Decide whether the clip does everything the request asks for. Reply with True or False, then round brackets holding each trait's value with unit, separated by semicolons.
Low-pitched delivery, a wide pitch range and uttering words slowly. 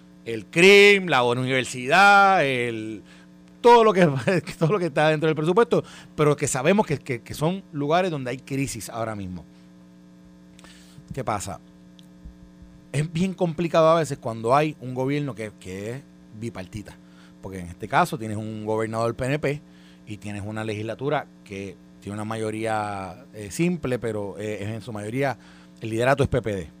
False (115 Hz; 7.9 semitones; 160 wpm)